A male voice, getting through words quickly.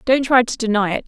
No: female; fast, 280 wpm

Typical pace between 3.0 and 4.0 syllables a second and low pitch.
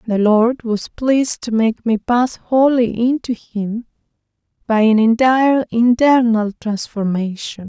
No: 3.9 syllables/s; high, 230 Hz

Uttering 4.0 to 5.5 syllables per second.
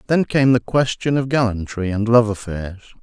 Yes: 5.0 syllables/s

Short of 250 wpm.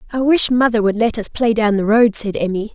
No: fast, 265 wpm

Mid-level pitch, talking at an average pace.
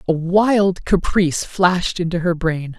Yes: medium, 175 Hz; average, 150 wpm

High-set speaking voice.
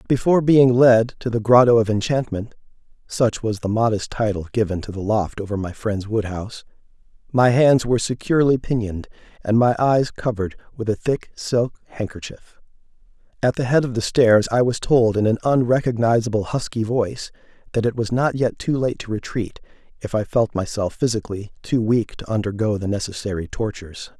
No: low, 115 Hz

